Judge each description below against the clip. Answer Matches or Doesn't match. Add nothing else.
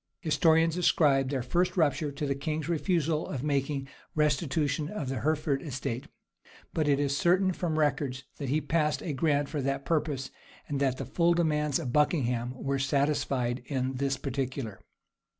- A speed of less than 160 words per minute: Doesn't match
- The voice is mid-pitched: Matches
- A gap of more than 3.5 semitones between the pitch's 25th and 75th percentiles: Doesn't match